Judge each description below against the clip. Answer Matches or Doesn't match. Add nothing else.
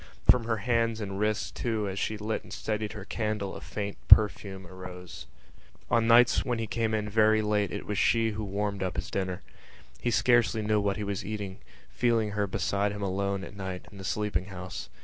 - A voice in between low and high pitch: Doesn't match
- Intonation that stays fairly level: Matches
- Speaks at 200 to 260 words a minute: Matches